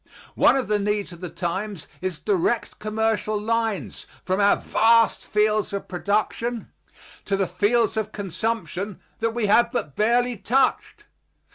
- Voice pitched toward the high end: Yes, high, 215 Hz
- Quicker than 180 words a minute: No, average, 145 wpm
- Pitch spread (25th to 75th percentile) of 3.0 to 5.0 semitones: No, narrow, 2.5 semitones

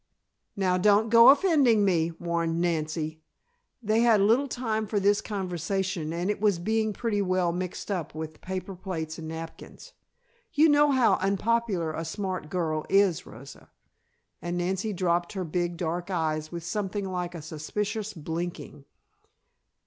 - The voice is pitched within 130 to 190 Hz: Yes, medium, 185 Hz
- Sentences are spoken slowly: No, average, 150 wpm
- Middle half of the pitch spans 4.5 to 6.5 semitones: No, average, 3.9 semitones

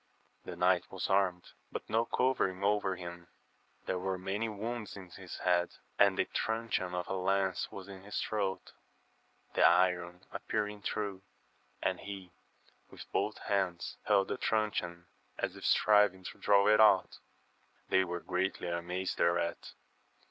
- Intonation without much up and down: Yes, narrow, 2.3 semitones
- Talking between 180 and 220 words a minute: No, average, 155 wpm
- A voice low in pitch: Yes, very low, 95 Hz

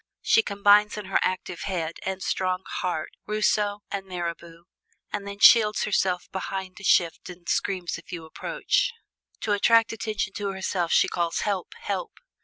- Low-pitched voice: No, high, 190 Hz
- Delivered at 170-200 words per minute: No, average, 160 wpm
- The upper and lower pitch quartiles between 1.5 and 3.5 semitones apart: Yes, narrow, 2.6 semitones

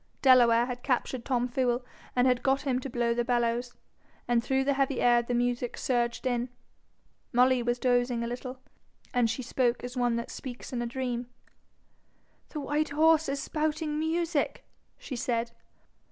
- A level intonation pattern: Yes, narrow, 1.9 semitones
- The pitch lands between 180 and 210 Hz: No, high, 245 Hz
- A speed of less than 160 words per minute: No, average, 165 wpm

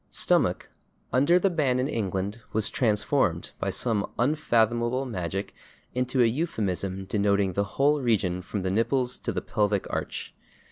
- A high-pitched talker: No, low, 115 Hz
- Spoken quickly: No, average, 145 wpm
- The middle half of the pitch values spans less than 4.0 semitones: No, average, 4.5 semitones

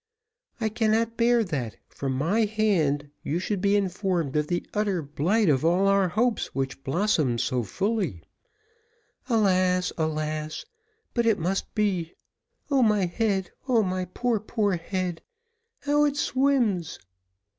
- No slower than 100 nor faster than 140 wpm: Yes, slow, 135 wpm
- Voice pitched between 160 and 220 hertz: Yes, high, 190 Hz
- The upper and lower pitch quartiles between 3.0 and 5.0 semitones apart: No, wide, 5.5 semitones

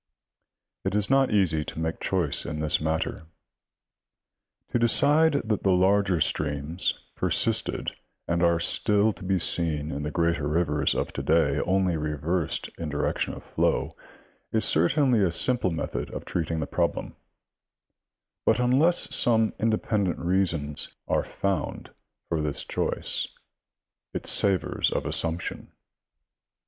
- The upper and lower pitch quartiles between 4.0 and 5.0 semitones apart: Yes, average, 4.7 semitones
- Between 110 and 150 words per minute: Yes, slow, 135 wpm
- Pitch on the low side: Yes, very low, 85 Hz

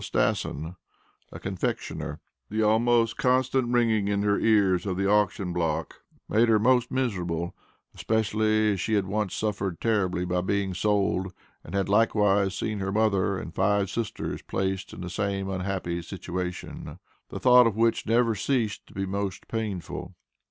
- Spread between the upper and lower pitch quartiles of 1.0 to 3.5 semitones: Yes, average, 2.8 semitones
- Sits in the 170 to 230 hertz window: No, low, 100 Hz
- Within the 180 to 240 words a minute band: No, average, 155 wpm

